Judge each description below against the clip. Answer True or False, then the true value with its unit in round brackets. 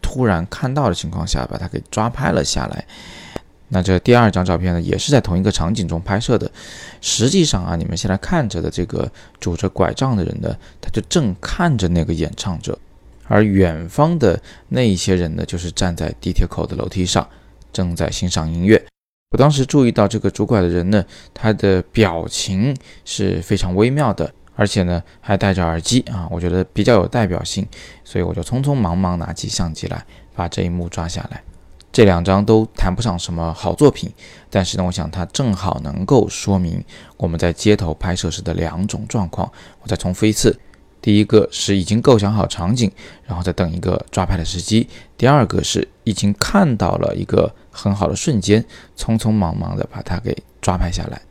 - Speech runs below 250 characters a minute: False (290 characters per minute)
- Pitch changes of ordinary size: True (3.8 semitones)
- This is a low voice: True (95 Hz)